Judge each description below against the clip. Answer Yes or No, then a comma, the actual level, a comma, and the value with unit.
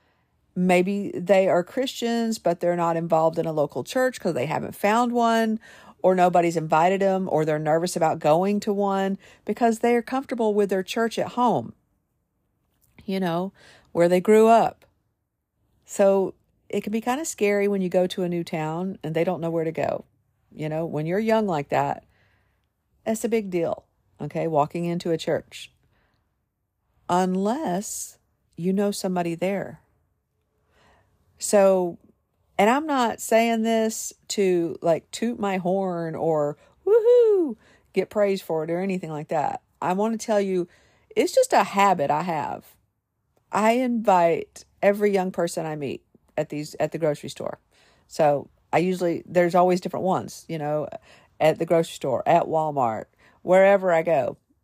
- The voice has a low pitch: No, medium, 180 Hz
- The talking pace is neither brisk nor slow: Yes, average, 165 wpm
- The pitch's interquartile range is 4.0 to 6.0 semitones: Yes, average, 4.5 semitones